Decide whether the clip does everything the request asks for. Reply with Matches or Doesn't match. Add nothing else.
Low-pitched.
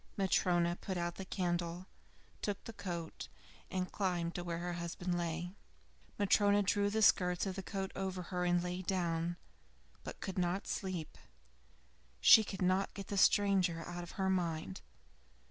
Doesn't match